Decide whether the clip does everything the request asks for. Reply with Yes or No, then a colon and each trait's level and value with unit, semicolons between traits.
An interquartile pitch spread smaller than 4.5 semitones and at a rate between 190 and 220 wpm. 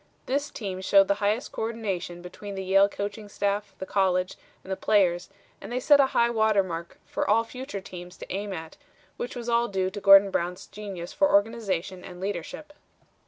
Yes: average, 3.0 semitones; average, 195 wpm